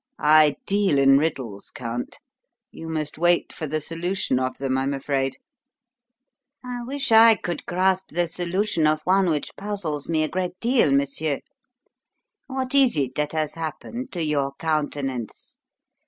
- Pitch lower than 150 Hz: No, medium, 155 Hz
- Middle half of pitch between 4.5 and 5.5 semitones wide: Yes, average, 5.0 semitones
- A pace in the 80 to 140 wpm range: No, average, 150 wpm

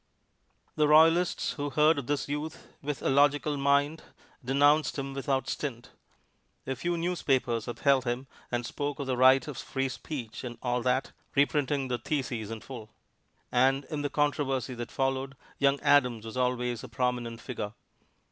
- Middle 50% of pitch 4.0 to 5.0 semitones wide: No, average, 2.7 semitones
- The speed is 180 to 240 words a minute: No, average, 160 wpm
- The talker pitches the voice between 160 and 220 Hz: No, low, 135 Hz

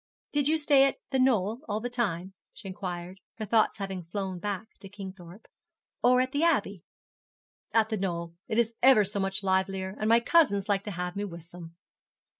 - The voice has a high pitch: Yes, high, 200 Hz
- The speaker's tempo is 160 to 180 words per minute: No, average, 195 wpm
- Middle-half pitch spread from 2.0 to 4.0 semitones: Yes, average, 3.7 semitones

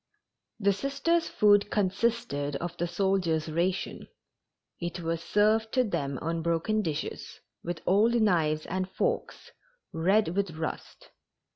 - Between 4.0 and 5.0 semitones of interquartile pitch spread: Yes, average, 4.5 semitones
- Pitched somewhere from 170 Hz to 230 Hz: Yes, medium, 185 Hz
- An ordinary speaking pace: No, slow, 125 wpm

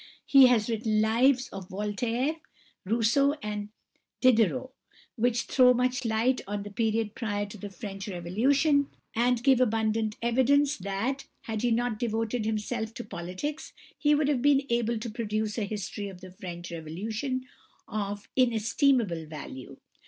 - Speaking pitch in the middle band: No, high, 225 Hz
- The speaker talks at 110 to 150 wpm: Yes, average, 145 wpm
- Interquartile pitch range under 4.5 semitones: Yes, average, 3.6 semitones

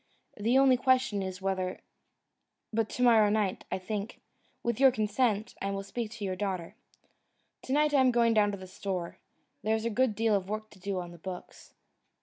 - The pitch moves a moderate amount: Yes, average, 3.5 semitones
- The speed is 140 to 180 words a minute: No, average, 200 wpm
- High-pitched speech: Yes, high, 210 Hz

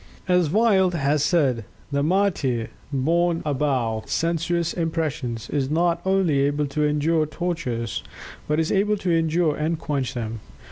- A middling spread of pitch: Yes, average, 3.7 semitones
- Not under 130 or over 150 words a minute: Yes, average, 140 wpm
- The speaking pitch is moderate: Yes, medium, 155 Hz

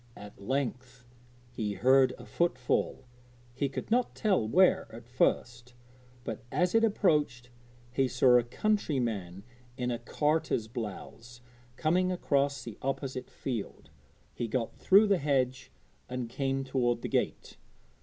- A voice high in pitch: No, low, 130 Hz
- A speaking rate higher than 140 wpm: No, slow, 135 wpm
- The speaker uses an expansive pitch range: No, average, 3.5 semitones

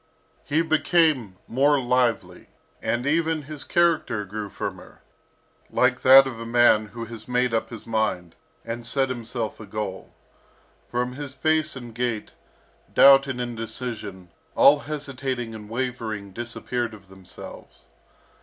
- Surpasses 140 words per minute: No, slow, 135 wpm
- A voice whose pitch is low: Yes, low, 120 Hz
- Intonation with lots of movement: No, average, 3.6 semitones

